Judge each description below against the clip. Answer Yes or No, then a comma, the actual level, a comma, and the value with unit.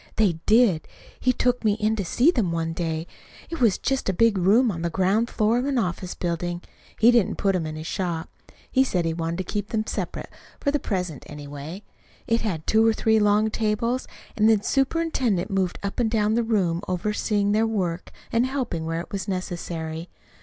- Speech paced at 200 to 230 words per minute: Yes, fast, 205 wpm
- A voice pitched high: Yes, high, 205 Hz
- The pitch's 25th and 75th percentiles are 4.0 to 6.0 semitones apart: Yes, average, 4.7 semitones